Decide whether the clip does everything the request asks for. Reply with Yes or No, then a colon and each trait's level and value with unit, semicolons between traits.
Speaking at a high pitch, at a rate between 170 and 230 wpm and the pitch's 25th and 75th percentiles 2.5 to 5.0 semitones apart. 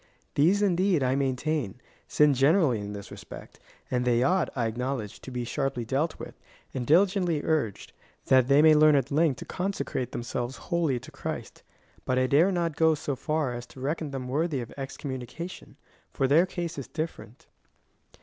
No: medium, 140 Hz; average, 175 wpm; average, 4.3 semitones